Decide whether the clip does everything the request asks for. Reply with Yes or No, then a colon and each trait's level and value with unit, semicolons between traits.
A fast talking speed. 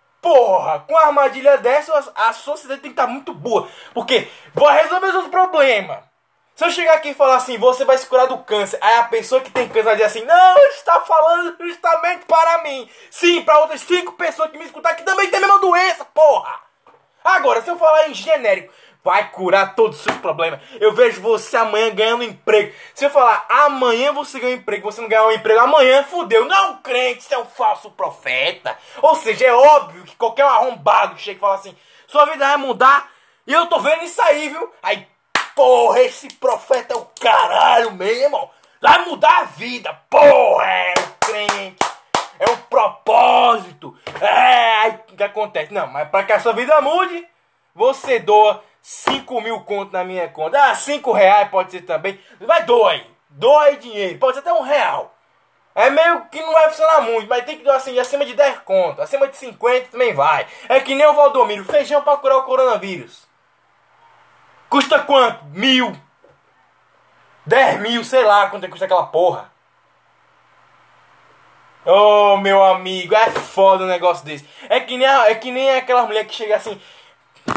Yes: fast, 190 wpm